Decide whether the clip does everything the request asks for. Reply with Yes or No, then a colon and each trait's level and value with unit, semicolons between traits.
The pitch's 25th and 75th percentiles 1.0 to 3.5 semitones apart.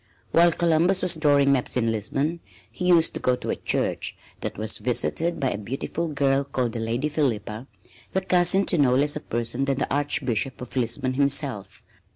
No: average, 4.6 semitones